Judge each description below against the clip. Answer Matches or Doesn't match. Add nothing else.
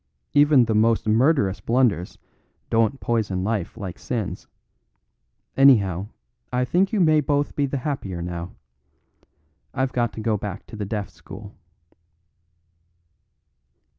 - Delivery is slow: Matches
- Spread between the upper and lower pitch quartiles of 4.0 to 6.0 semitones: Matches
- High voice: Doesn't match